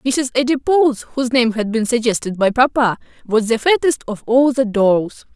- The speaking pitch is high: Yes, high, 240 Hz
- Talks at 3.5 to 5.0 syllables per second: Yes, 4.9 syllables/s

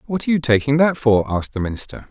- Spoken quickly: Yes, fast, 255 wpm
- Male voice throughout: Yes, male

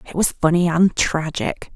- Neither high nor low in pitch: Yes, medium, 165 Hz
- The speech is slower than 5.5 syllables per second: Yes, 4.5 syllables/s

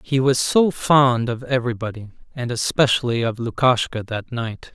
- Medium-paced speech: Yes, average, 150 wpm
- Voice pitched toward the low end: Yes, low, 125 Hz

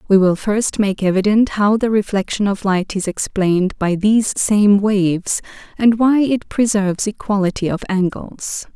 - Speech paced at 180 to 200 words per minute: No, average, 160 wpm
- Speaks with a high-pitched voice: Yes, high, 205 Hz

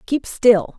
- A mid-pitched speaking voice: No, high, 230 Hz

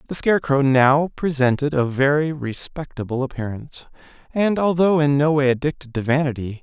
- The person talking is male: Yes, male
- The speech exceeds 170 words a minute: No, average, 155 wpm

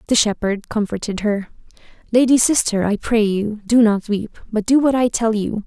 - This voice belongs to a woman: Yes, female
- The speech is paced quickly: No, average, 190 wpm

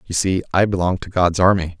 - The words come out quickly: Yes, fast, 235 wpm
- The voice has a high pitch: No, very low, 90 Hz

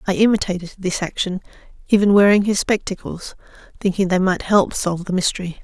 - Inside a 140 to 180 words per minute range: Yes, average, 160 wpm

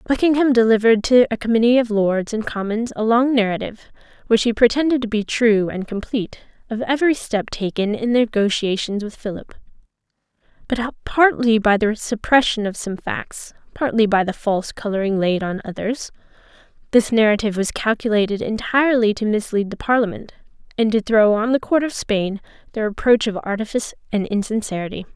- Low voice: No, high, 220 Hz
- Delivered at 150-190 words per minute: Yes, average, 160 wpm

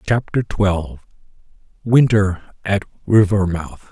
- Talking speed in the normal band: No, slow, 60 wpm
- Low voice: Yes, low, 100 Hz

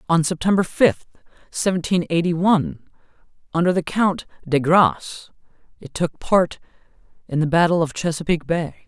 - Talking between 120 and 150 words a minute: Yes, slow, 135 wpm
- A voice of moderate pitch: Yes, medium, 165 Hz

